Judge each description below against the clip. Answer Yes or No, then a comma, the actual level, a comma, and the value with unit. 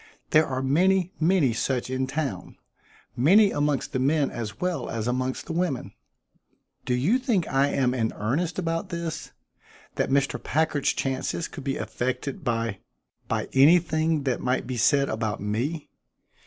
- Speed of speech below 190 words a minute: Yes, average, 155 wpm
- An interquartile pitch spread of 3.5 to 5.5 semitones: Yes, average, 4.5 semitones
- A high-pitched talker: No, medium, 140 Hz